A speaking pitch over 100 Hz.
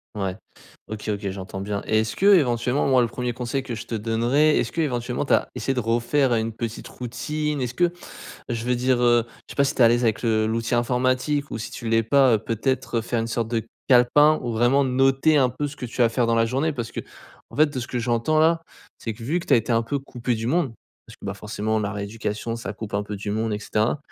Yes: low, 120 Hz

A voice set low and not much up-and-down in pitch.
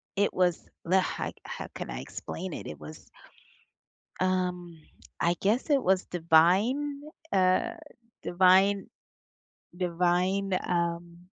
No: medium, 180 Hz; narrow, 2.0 semitones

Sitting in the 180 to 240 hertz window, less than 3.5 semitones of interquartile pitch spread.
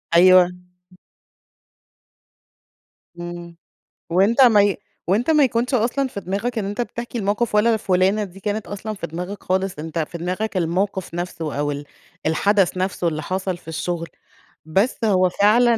No: high, 190 Hz; average, 3.8 semitones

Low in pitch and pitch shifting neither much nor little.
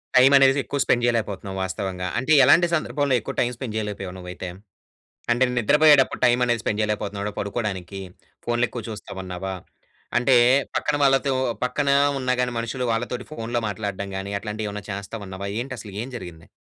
Yes: low, 115 Hz; average, 4.2 semitones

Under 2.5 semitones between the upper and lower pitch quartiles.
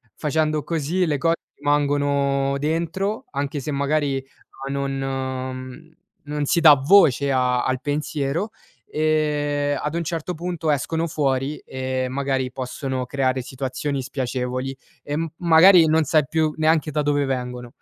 No: average, 2.8 semitones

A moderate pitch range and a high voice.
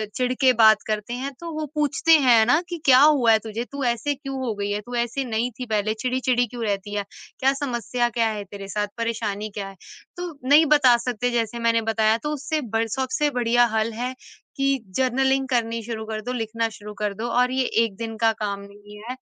Yes: average, 3.1 semitones; high, 235 Hz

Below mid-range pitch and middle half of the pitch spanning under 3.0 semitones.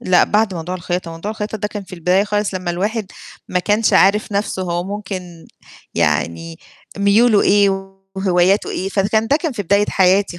No: high, 195 Hz; narrow, 2.4 semitones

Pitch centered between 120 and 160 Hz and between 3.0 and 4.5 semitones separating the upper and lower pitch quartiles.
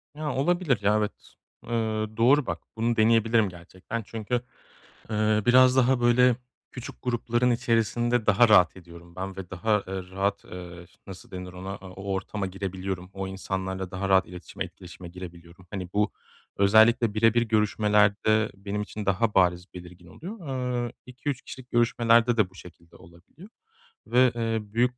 No: low, 105 Hz; average, 4.0 semitones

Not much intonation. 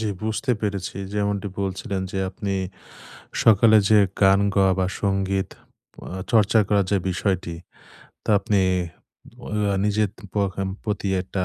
Yes: narrow, 1.5 semitones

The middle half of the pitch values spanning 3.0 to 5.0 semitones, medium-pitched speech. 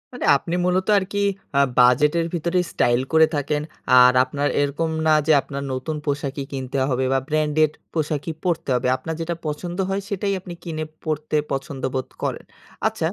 Yes: average, 3.5 semitones; medium, 150 Hz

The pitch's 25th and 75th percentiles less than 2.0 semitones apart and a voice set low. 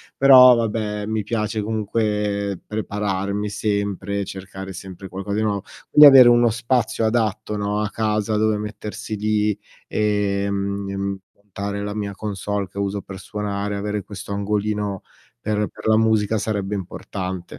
Yes: narrow, 1.3 semitones; low, 105 Hz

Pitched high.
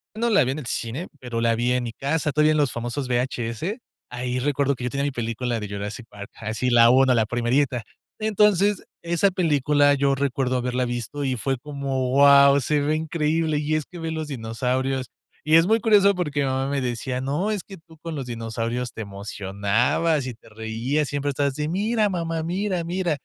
No: medium, 140 Hz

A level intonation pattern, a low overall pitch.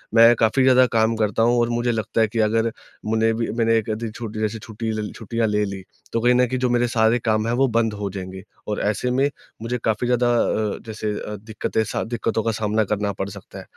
Yes: narrow, 1.7 semitones; low, 110 Hz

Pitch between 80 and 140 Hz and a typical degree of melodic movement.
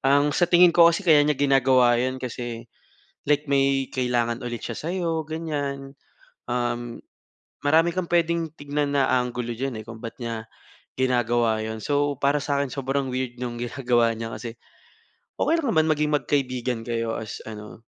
Yes: low, 135 Hz; average, 3.6 semitones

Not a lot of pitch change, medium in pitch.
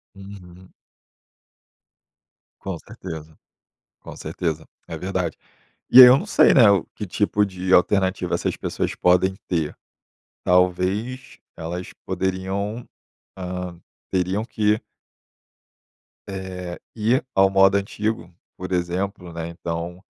No: narrow, 2.2 semitones; very low, 95 Hz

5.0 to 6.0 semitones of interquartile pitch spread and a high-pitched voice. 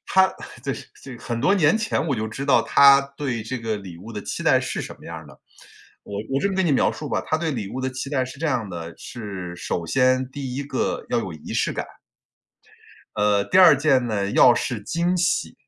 No: average, 5.3 semitones; low, 130 Hz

